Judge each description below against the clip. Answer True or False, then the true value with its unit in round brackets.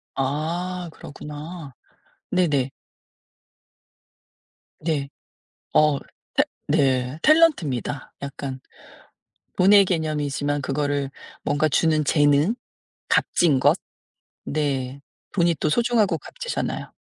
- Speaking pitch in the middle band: True (150 Hz)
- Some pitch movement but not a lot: True (3.8 semitones)